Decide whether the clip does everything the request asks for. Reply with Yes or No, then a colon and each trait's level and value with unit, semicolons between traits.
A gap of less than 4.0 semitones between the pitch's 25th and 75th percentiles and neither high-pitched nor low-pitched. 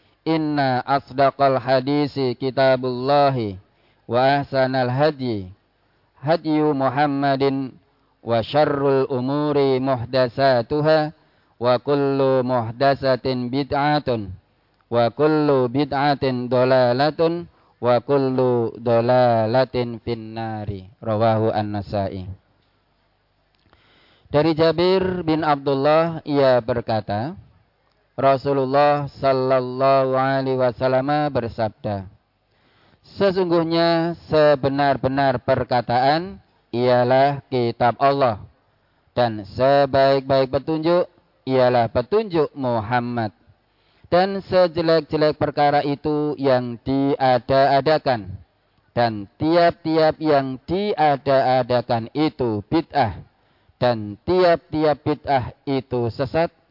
No: average, 3.6 semitones; low, 130 Hz